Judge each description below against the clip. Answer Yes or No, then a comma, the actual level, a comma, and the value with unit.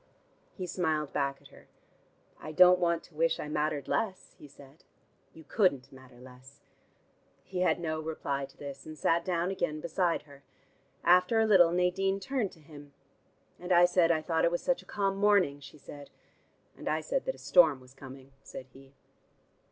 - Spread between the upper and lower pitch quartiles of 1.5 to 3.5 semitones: No, average, 4.3 semitones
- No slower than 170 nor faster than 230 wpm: Yes, average, 185 wpm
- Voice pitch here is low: No, medium, 160 Hz